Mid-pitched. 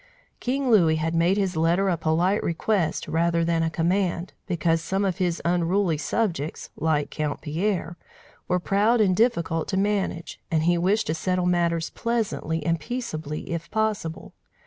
Yes: medium, 175 Hz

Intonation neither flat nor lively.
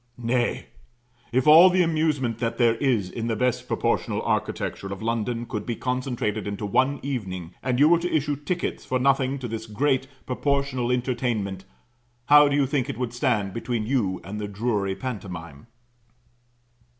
Yes: average, 4.4 semitones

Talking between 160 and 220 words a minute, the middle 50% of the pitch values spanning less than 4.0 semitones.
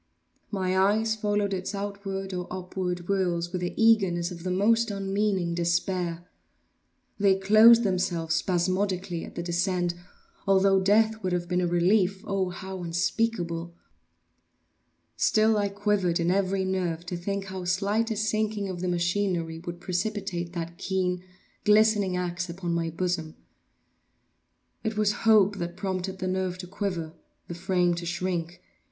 No: average, 145 wpm; narrow, 2.4 semitones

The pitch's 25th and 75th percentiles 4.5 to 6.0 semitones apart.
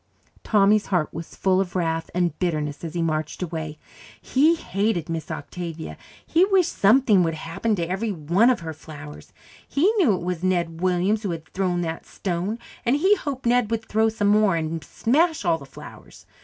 Yes: average, 5.2 semitones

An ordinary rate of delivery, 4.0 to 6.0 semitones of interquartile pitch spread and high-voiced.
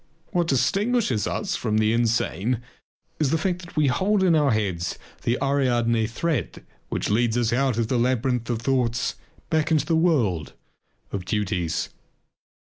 No: average, 155 wpm; wide, 5.6 semitones; low, 125 Hz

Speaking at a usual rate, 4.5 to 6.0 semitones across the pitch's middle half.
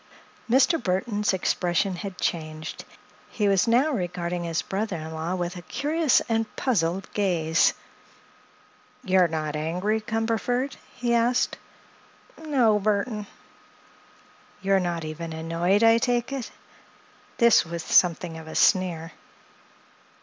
No: slow, 120 wpm; average, 5.3 semitones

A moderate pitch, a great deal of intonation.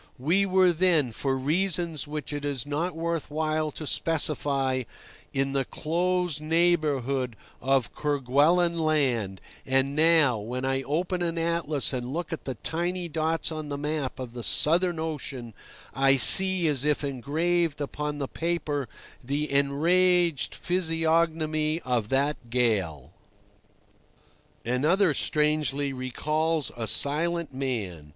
No: medium, 150 Hz; average, 3.7 semitones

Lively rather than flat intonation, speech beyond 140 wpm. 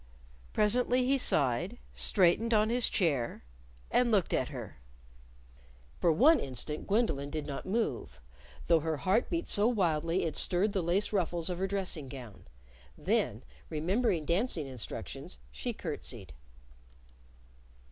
No: wide, 6.2 semitones; slow, 135 wpm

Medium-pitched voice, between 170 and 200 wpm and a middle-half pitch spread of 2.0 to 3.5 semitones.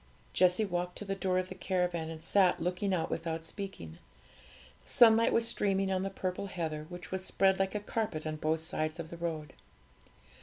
Yes: medium, 180 Hz; average, 195 wpm; average, 3.0 semitones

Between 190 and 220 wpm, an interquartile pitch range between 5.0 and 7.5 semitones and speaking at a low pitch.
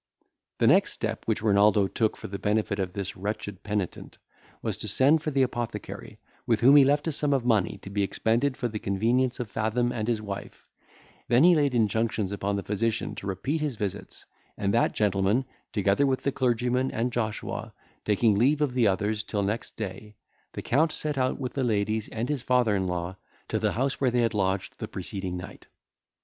No: average, 200 wpm; average, 4.0 semitones; low, 110 Hz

